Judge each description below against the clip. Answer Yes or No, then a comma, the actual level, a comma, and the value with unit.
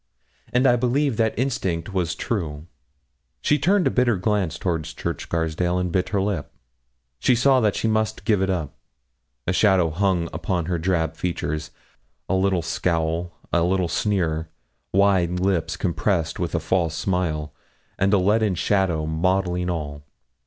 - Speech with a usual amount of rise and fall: Yes, average, 3.6 semitones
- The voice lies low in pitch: Yes, very low, 90 Hz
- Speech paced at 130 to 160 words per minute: Yes, average, 155 wpm